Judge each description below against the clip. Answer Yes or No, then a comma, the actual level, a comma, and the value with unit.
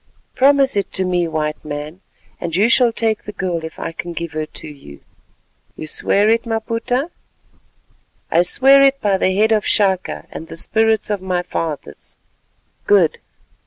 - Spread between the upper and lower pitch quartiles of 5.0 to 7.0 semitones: Yes, average, 5.3 semitones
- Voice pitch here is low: No, high, 190 Hz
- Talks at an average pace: Yes, average, 165 wpm